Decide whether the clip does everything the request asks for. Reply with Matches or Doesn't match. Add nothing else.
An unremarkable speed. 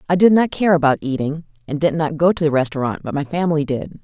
Doesn't match